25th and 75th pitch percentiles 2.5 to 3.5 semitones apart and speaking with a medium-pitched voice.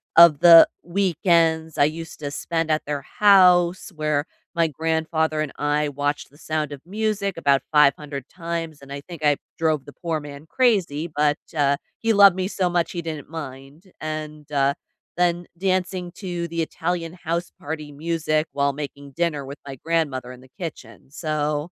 Yes: average, 2.8 semitones; medium, 155 Hz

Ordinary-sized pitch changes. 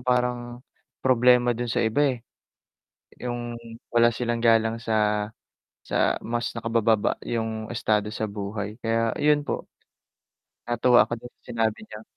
No: narrow, 1.7 semitones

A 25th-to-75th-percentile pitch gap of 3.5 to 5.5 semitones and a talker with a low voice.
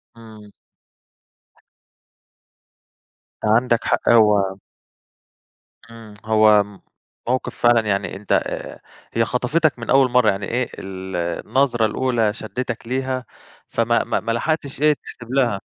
No: average, 3.0 semitones; low, 115 Hz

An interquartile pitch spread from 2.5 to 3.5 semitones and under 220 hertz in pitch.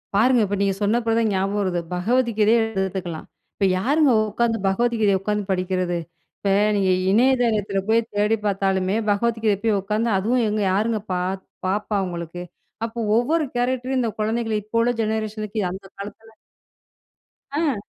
Yes: average, 3.2 semitones; high, 210 Hz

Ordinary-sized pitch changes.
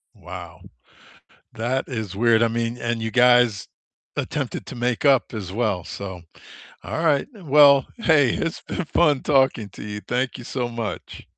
Yes: average, 3.7 semitones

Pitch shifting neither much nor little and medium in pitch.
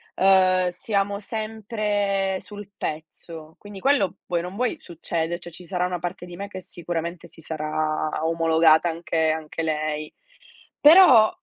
Yes: average, 3.7 semitones; medium, 175 Hz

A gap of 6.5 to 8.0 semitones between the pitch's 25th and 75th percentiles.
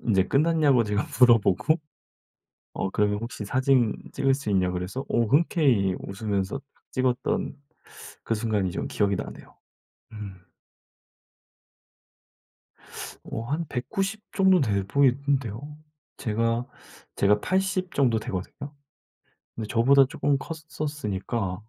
No: wide, 5.5 semitones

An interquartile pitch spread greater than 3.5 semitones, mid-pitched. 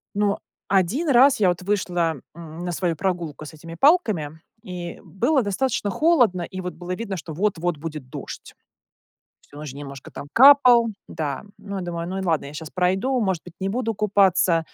Yes: average, 4.2 semitones; medium, 180 Hz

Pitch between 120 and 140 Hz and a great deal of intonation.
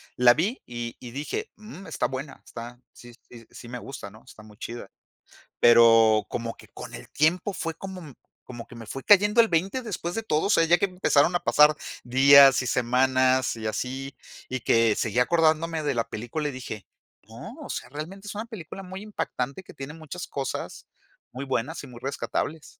Yes: low, 135 Hz; wide, 6.1 semitones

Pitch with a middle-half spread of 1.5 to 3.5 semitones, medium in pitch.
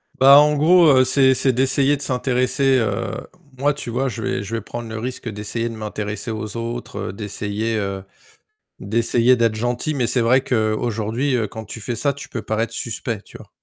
No: average, 3.2 semitones; low, 120 Hz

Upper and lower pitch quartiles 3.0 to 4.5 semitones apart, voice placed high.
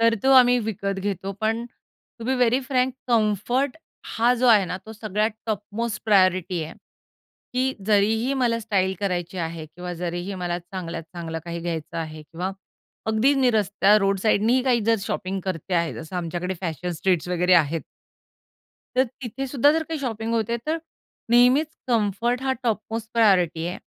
No: average, 4.9 semitones; high, 205 Hz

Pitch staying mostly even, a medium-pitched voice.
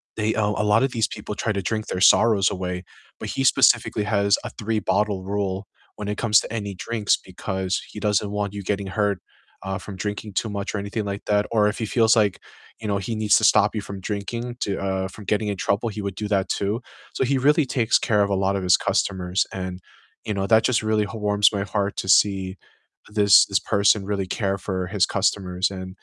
No: narrow, 1.8 semitones; low, 100 Hz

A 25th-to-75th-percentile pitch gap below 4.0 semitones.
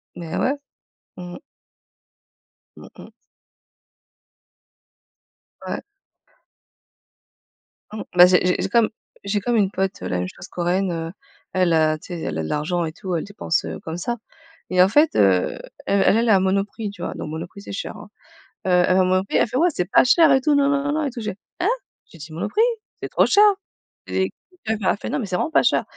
No: average, 4.7 semitones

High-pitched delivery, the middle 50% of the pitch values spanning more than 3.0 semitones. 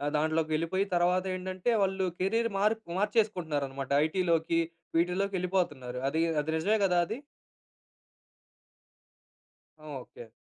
No: medium, 180 Hz; average, 3.5 semitones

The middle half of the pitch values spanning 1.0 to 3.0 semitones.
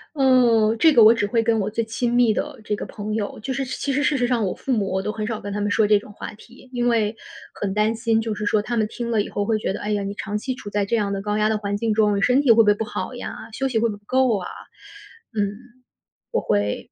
Yes: narrow, 2.5 semitones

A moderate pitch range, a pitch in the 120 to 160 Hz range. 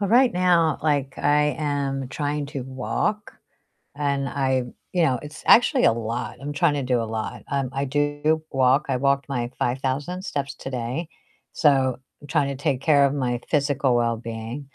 No: narrow, 2.3 semitones; medium, 140 Hz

